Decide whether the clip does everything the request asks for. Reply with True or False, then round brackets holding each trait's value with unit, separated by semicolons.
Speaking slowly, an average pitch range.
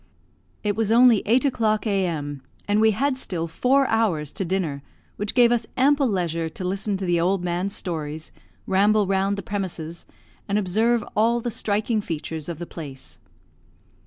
False (165 wpm; 4.6 semitones)